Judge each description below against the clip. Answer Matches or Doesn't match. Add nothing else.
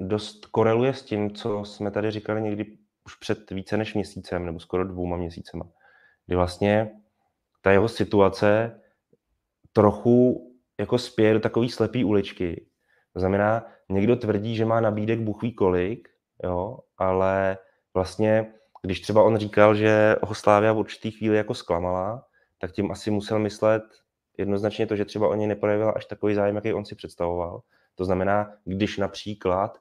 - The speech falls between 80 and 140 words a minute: Doesn't match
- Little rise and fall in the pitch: Matches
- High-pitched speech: Doesn't match